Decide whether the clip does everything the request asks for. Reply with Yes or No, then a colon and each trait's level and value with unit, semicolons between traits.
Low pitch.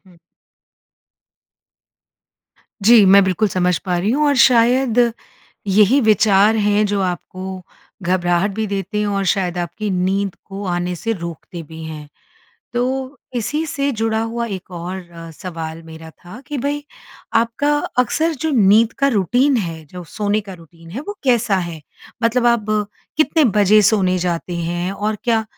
No: high, 200 Hz